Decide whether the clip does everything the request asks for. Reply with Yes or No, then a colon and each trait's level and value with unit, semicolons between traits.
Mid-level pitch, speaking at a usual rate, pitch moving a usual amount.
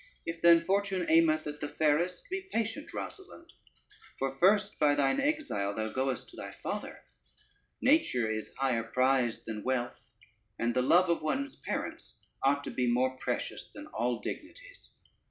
No: medium, 150 Hz; average, 155 wpm; wide, 7.9 semitones